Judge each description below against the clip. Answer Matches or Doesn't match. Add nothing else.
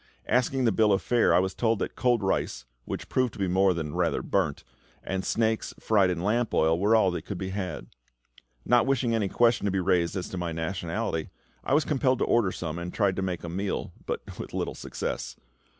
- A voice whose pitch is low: Matches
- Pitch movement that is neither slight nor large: Matches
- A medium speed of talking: Doesn't match